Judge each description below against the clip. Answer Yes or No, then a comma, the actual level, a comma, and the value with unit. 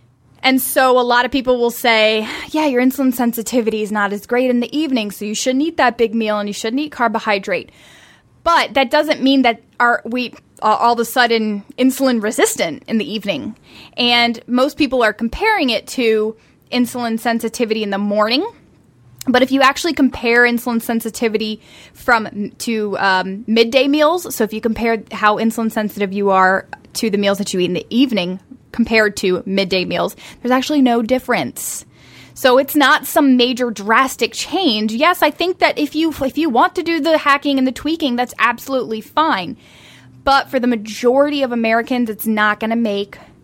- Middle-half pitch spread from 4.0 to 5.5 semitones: No, average, 3.6 semitones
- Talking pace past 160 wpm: Yes, average, 185 wpm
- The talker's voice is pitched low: No, high, 240 Hz